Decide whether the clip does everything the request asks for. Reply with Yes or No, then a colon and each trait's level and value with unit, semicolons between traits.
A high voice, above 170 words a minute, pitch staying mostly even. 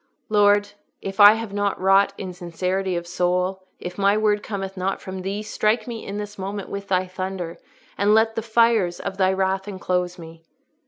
Yes: high, 195 Hz; average, 190 wpm; narrow, 2.0 semitones